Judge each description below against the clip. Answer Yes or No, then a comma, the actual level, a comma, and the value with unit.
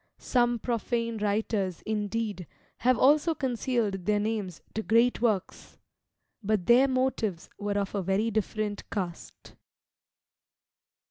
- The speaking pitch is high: Yes, high, 220 Hz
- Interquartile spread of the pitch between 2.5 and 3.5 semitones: Yes, average, 2.9 semitones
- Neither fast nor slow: No, slow, 115 wpm